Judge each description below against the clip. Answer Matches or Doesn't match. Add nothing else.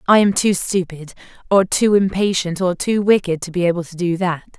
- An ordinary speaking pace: Doesn't match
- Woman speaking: Matches